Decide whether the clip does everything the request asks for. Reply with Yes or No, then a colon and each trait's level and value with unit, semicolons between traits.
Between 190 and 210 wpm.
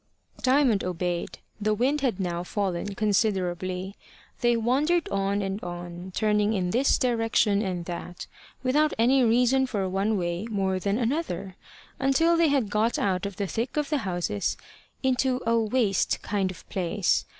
No: average, 155 wpm